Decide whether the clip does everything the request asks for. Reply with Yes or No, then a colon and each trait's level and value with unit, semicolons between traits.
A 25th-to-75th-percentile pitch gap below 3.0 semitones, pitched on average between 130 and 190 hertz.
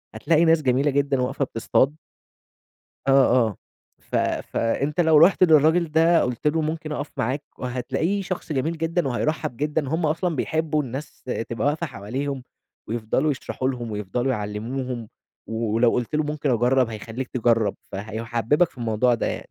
No: average, 4.6 semitones; low, 135 Hz